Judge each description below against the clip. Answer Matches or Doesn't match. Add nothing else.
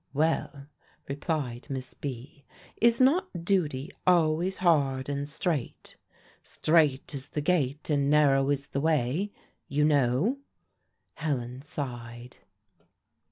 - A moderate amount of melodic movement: Matches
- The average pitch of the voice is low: Doesn't match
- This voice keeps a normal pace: Doesn't match